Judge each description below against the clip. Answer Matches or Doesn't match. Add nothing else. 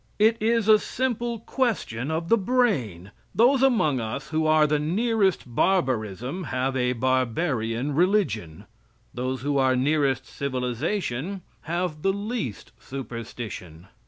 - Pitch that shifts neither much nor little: Doesn't match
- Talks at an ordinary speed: Doesn't match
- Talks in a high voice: Doesn't match